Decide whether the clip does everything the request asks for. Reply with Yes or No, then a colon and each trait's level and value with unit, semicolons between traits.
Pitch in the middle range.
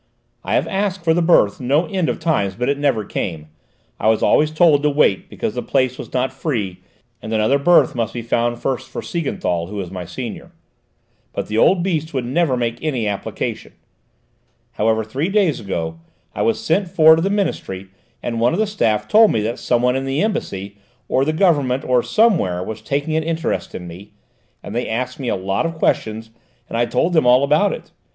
No: low, 130 Hz